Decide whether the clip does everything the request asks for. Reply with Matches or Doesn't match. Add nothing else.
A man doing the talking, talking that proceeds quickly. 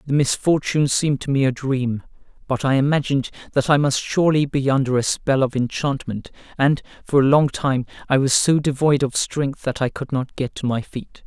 Matches